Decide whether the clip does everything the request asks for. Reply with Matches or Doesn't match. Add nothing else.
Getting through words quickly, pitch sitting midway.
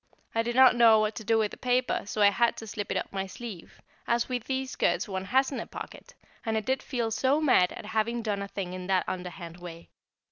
Doesn't match